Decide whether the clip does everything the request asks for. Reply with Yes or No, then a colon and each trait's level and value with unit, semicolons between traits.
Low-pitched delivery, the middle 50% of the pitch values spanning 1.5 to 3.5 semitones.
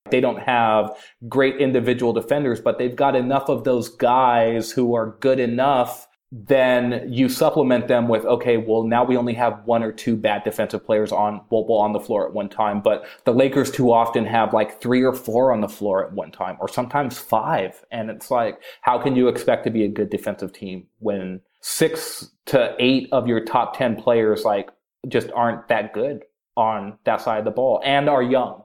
Yes: low, 120 Hz; narrow, 2.4 semitones